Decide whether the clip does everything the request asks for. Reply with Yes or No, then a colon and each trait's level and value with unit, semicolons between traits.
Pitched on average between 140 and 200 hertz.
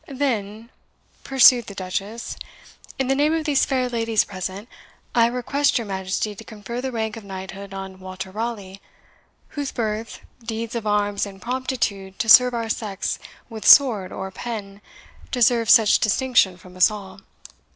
No: high, 220 Hz